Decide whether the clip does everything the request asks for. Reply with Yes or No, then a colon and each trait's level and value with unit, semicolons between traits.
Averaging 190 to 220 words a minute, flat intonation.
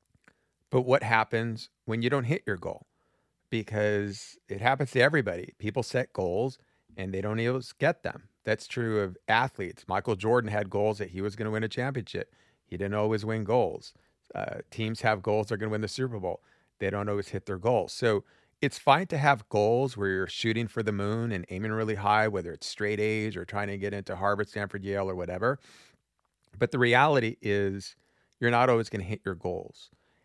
Yes: fast, 205 wpm; narrow, 2.3 semitones